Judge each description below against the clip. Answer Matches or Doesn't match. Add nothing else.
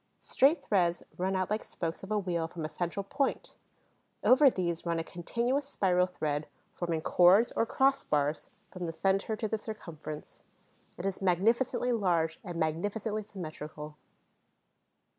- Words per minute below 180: Matches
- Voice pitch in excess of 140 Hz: Matches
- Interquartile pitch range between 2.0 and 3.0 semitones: Doesn't match